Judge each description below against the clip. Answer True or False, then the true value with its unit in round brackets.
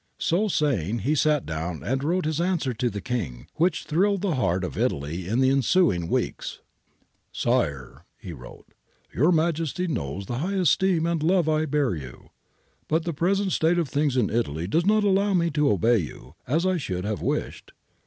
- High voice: False (145 Hz)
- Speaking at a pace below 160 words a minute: False (195 wpm)